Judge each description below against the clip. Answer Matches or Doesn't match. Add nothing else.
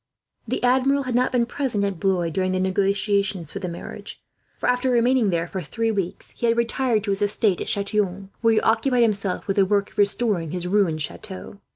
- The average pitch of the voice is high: Matches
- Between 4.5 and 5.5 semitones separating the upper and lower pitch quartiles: Doesn't match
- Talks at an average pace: Doesn't match